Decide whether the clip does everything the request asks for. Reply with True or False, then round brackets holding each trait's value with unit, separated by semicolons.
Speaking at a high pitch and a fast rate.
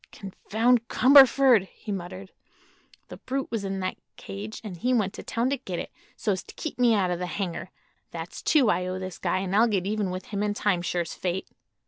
True (200 Hz; 210 wpm)